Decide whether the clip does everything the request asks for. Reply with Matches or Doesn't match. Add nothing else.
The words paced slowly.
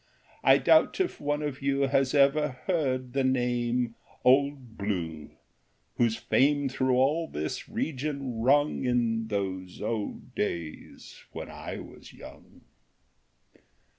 Matches